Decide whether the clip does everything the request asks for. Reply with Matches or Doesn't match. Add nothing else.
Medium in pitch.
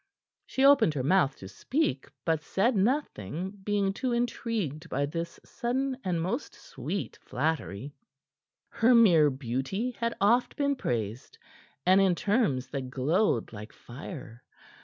Matches